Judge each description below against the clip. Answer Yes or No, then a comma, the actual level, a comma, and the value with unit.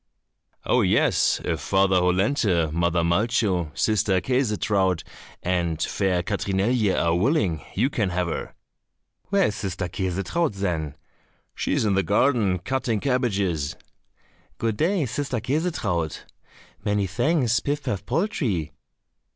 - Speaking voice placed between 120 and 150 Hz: No, low, 100 Hz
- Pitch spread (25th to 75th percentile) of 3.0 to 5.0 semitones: No, wide, 5.6 semitones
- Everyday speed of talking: No, slow, 120 wpm